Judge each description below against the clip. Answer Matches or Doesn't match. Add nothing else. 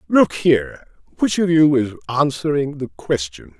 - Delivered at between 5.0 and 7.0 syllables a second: Doesn't match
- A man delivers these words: Matches